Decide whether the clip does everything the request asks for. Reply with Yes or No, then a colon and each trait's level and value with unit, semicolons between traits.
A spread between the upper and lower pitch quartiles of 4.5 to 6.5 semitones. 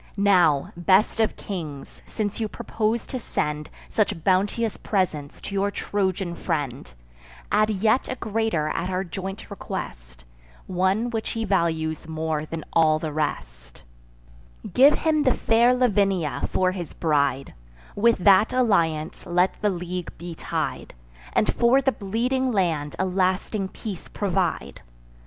Yes: average, 5.1 semitones